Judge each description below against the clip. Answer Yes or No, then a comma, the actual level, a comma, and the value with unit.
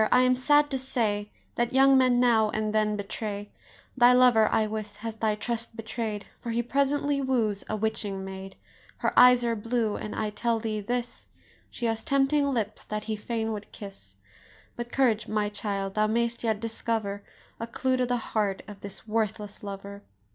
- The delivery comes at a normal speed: Yes, average, 185 wpm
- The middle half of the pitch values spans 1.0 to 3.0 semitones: Yes, average, 2.7 semitones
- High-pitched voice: Yes, high, 225 Hz